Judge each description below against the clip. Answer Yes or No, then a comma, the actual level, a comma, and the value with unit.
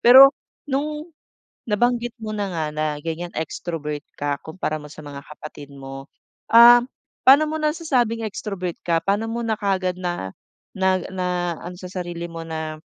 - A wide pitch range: Yes, wide, 6.7 semitones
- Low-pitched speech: No, medium, 185 Hz